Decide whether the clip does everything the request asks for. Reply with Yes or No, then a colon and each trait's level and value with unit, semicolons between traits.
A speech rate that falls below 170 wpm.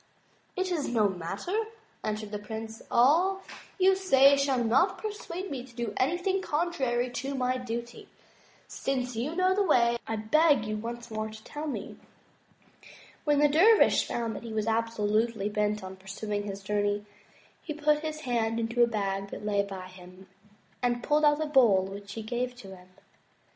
No: average, 175 wpm